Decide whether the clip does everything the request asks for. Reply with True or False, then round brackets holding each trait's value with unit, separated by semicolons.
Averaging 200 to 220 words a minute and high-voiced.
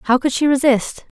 True (205 wpm; 265 Hz)